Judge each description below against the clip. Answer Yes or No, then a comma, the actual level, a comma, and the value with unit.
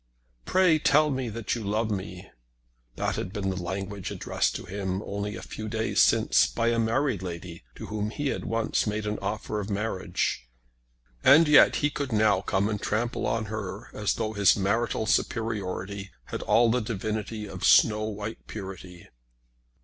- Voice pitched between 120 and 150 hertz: No, low, 105 Hz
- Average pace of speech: Yes, average, 170 wpm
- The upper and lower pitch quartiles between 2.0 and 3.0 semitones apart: Yes, average, 2.7 semitones